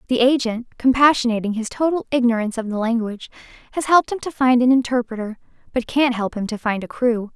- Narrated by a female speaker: Yes, female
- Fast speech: No, average, 195 wpm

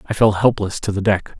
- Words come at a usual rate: No, fast, 260 wpm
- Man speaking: Yes, male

